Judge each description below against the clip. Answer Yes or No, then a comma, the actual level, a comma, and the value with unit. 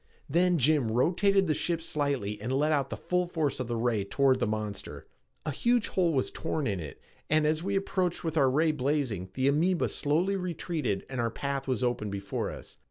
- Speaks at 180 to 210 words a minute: Yes, fast, 205 wpm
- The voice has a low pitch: No, medium, 145 Hz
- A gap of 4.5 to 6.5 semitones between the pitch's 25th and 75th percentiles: Yes, wide, 5.5 semitones